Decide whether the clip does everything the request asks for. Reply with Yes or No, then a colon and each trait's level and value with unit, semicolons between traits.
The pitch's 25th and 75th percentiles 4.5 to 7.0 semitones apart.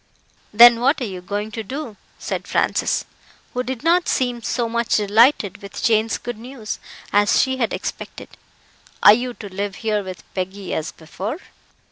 No: average, 3.3 semitones